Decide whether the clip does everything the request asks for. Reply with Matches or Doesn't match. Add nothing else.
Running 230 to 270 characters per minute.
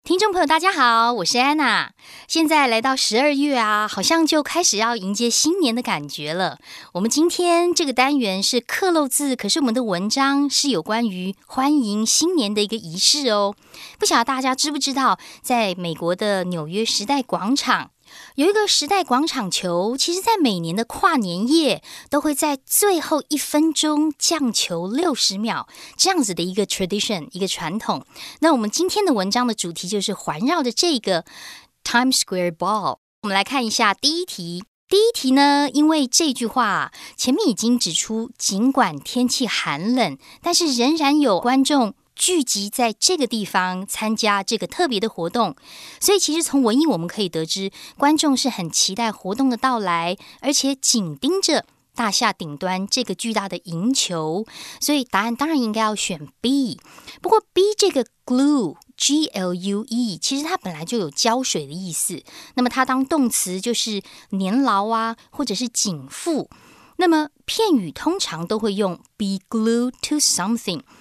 Doesn't match